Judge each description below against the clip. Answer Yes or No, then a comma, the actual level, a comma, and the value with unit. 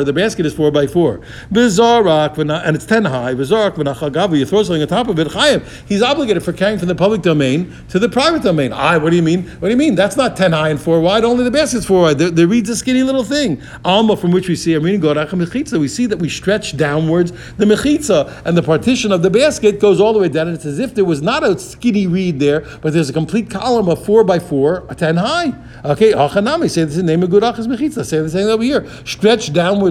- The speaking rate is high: Yes, fast, 240 wpm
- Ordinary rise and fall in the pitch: No, wide, 5.8 semitones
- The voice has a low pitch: No, medium, 185 Hz